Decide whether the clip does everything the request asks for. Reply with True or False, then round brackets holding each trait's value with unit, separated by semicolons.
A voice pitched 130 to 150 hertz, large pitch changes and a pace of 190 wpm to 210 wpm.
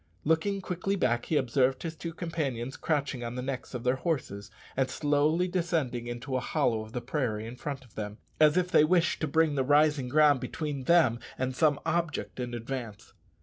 False (140 Hz; 4.5 semitones; 195 wpm)